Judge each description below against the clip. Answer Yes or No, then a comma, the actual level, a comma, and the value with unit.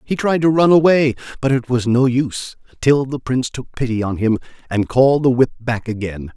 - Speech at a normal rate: No, fast, 215 wpm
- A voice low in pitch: Yes, low, 125 Hz